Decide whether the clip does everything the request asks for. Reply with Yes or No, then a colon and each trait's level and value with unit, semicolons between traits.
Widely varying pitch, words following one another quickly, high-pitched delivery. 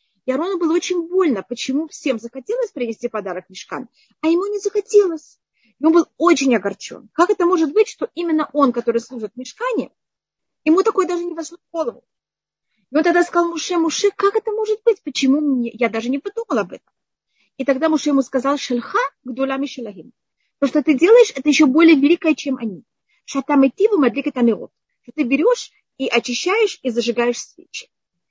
Yes: wide, 5.8 semitones; fast, 180 wpm; very high, 300 Hz